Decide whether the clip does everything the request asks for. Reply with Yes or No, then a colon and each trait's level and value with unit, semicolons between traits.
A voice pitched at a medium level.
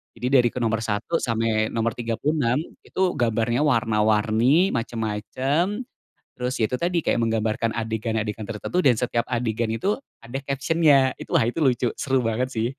No: low, 120 Hz